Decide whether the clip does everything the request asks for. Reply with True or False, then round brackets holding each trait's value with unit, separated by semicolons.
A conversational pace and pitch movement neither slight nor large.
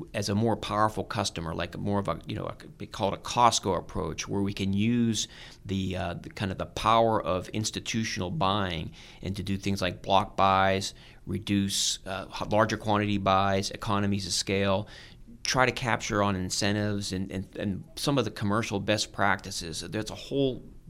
False (185 wpm; 2.2 semitones)